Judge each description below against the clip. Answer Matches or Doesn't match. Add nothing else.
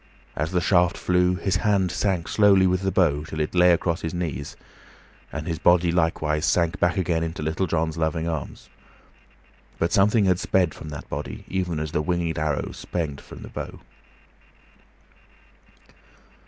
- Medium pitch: Doesn't match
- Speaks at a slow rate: Doesn't match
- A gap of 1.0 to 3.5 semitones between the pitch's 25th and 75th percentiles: Matches